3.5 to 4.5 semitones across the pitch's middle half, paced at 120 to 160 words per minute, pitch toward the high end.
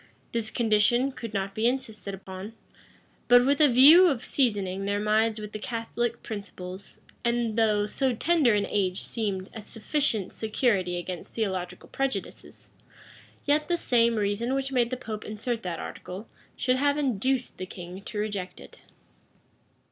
Yes: average, 4.0 semitones; average, 150 wpm; high, 220 Hz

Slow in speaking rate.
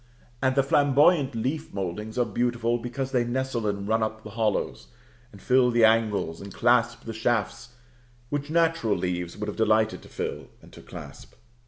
No: average, 175 wpm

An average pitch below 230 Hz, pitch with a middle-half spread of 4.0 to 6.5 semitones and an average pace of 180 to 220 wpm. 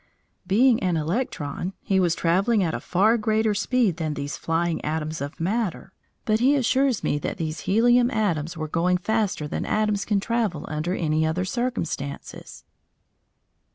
No: medium, 185 Hz; wide, 5.6 semitones; average, 155 wpm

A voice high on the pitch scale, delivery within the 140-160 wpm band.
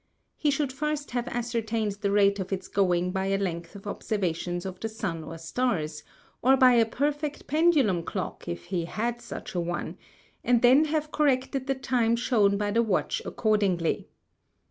No: high, 220 Hz; average, 175 wpm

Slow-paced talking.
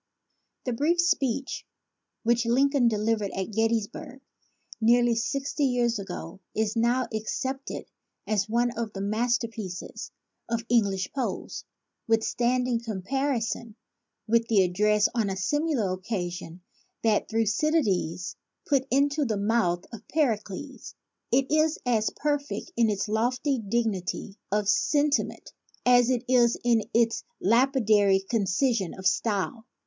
Yes: slow, 125 wpm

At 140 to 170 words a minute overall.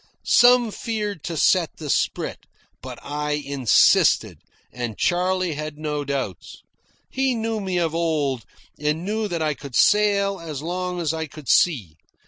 Yes: average, 150 wpm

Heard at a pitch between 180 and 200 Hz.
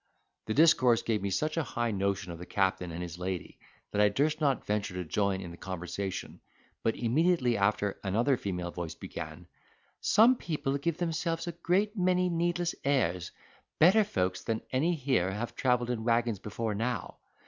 No: low, 115 Hz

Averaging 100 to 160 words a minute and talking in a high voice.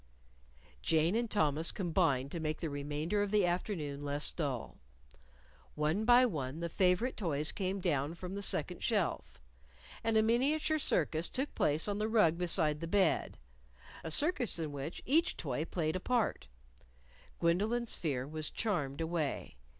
No: average, 155 wpm; medium, 170 Hz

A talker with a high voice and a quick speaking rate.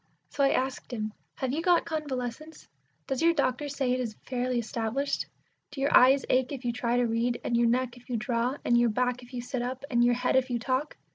Yes: very high, 250 Hz; fast, 235 wpm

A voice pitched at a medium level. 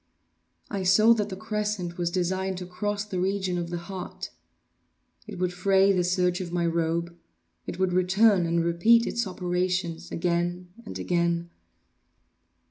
Yes: medium, 180 Hz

